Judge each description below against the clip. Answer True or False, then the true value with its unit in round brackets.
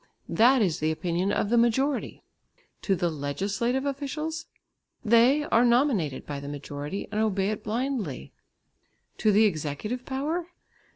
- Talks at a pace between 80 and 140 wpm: True (135 wpm)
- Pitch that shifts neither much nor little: False (7.8 semitones)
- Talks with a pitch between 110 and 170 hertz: False (215 Hz)